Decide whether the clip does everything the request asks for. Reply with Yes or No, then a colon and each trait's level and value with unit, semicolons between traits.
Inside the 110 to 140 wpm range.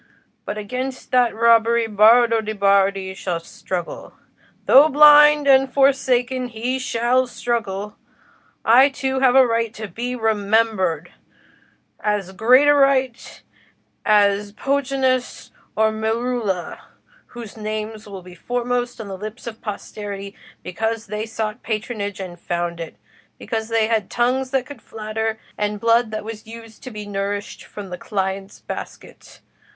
Yes: slow, 135 wpm